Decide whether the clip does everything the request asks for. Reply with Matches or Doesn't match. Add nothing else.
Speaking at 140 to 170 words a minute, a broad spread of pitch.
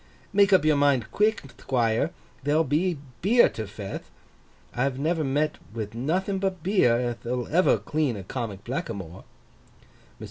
Matches